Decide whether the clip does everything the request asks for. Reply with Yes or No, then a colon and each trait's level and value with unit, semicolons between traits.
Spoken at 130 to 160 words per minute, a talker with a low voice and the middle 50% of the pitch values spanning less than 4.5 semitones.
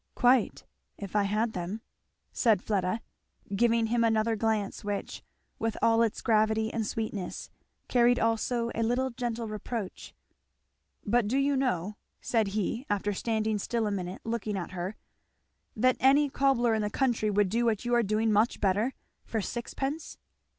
No: average, 155 wpm; high, 225 Hz; narrow, 2.4 semitones